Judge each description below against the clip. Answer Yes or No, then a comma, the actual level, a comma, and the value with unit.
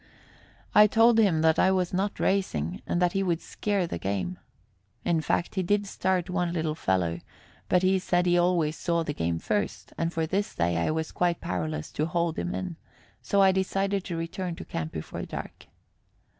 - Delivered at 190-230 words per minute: Yes, average, 195 wpm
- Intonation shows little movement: No, average, 3.5 semitones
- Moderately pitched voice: Yes, medium, 175 Hz